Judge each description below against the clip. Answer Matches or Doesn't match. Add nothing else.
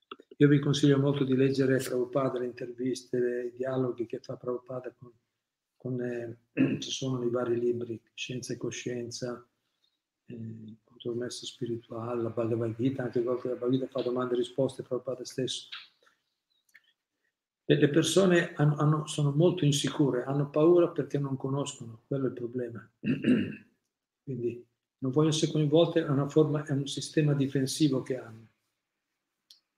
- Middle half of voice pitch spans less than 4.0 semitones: Matches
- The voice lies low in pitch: Matches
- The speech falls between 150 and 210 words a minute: Doesn't match